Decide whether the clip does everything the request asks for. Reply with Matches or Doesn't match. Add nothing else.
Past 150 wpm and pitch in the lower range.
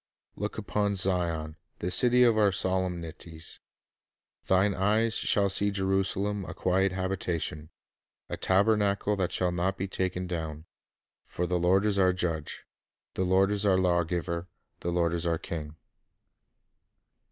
Doesn't match